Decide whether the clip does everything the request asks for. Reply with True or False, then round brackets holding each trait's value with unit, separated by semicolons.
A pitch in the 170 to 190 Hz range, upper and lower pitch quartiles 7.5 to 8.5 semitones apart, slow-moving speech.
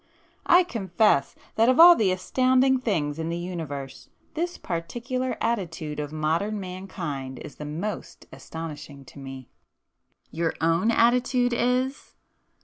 True (185 Hz; 8.1 semitones; 125 wpm)